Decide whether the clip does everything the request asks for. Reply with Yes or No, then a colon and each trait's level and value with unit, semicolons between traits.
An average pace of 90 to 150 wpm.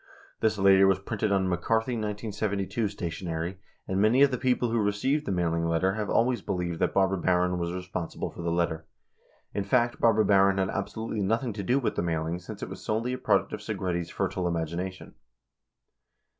No: average, 190 wpm